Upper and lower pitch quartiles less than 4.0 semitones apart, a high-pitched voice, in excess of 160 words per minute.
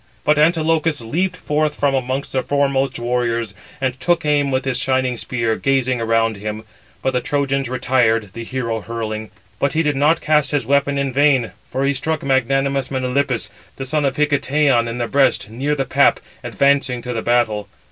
No: average, 3.0 semitones; low, 135 Hz; average, 185 wpm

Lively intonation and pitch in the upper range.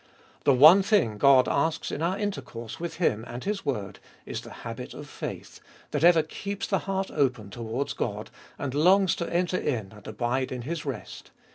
No: wide, 7.0 semitones; medium, 140 Hz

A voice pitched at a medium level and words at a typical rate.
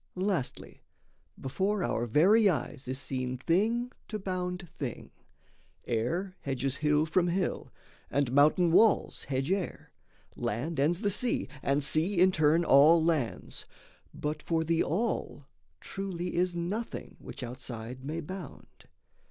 No: medium, 165 Hz; slow, 130 wpm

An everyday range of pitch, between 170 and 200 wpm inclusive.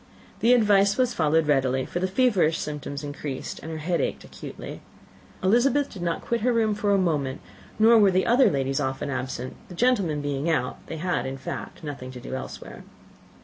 No: wide, 7.1 semitones; average, 190 wpm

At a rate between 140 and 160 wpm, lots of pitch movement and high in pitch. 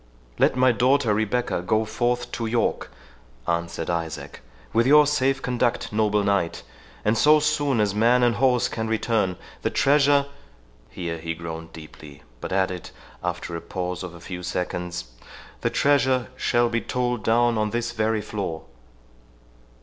No: average, 150 wpm; wide, 5.8 semitones; low, 110 Hz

